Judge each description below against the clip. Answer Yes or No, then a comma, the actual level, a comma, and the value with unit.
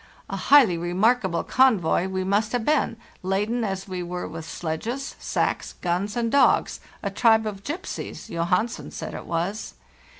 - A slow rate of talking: No, average, 155 wpm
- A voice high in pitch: Yes, high, 200 Hz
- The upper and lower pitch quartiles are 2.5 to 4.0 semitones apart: No, average, 4.8 semitones